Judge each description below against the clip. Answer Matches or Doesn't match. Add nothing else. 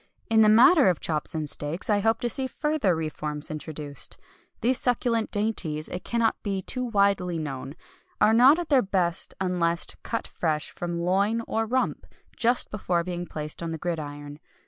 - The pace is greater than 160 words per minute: Matches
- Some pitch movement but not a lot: Doesn't match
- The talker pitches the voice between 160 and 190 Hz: Matches